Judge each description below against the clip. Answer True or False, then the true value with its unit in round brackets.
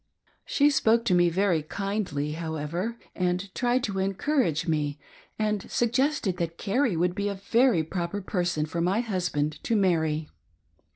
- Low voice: False (185 Hz)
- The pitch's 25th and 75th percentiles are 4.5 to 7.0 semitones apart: True (4.9 semitones)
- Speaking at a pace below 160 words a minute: True (150 wpm)